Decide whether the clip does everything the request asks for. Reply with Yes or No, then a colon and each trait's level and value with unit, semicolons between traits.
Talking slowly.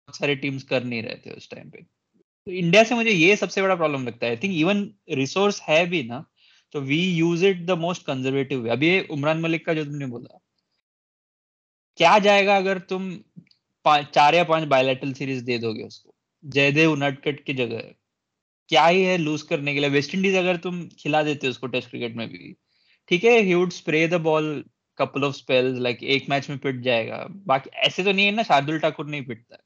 Yes: slow, 105 wpm